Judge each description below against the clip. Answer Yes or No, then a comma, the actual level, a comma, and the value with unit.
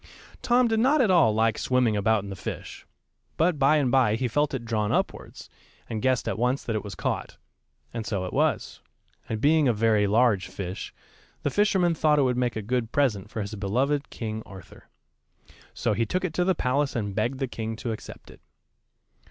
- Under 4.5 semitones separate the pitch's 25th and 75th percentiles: No, average, 5.1 semitones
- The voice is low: Yes, low, 120 Hz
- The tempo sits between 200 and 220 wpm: Yes, fast, 205 wpm